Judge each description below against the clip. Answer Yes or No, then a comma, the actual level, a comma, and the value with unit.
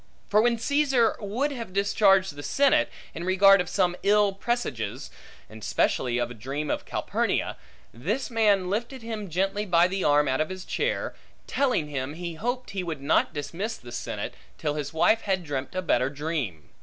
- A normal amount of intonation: No, wide, 6.6 semitones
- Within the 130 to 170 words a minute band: No, average, 180 wpm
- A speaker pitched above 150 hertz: Yes, medium, 185 Hz